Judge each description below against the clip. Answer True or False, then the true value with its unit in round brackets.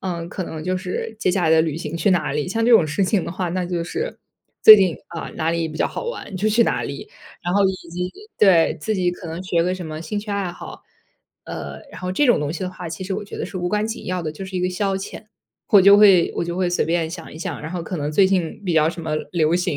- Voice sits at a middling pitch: True (180 Hz)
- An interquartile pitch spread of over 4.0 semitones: False (2.7 semitones)